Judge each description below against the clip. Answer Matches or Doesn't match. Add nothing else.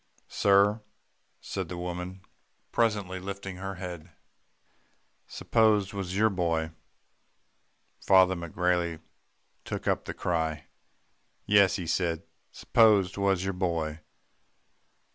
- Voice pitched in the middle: Doesn't match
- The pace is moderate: Doesn't match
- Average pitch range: Doesn't match